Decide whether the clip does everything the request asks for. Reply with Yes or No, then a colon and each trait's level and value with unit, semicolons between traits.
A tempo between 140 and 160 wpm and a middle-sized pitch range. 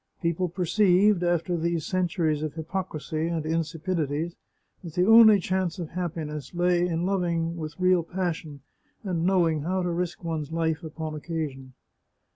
No: average, 145 wpm; narrow, 2.2 semitones